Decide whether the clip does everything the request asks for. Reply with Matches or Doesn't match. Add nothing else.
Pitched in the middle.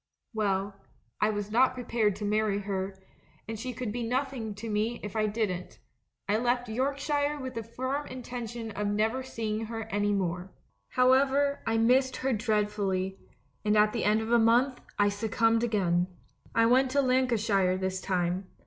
Doesn't match